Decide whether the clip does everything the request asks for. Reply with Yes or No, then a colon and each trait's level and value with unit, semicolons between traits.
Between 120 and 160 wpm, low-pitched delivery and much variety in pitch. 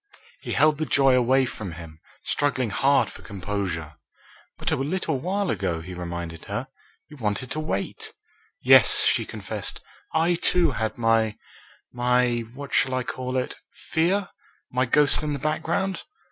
Yes: average, 155 wpm; low, 130 Hz; wide, 6.7 semitones